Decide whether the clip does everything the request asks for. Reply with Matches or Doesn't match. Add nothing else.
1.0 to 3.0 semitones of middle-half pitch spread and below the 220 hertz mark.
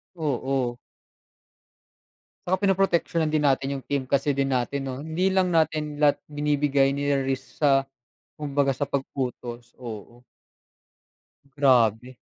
Matches